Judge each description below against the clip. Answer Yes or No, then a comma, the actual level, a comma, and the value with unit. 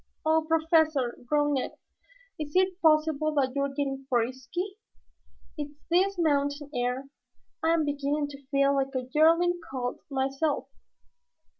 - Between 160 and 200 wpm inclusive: No, slow, 135 wpm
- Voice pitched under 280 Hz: No, very high, 290 Hz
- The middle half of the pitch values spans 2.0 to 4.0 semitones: Yes, average, 2.8 semitones